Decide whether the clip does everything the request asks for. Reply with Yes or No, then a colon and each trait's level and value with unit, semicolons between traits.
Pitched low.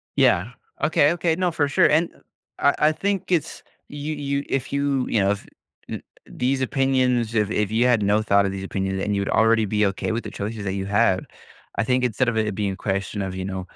Yes: low, 115 Hz